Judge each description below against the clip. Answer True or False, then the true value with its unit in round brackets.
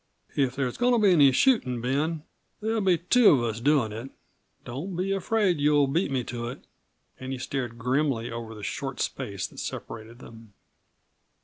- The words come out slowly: False (185 wpm)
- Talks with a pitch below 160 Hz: True (135 Hz)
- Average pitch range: False (6.8 semitones)